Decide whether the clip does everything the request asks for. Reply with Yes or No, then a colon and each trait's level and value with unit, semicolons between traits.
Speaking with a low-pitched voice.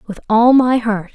No: high, 225 Hz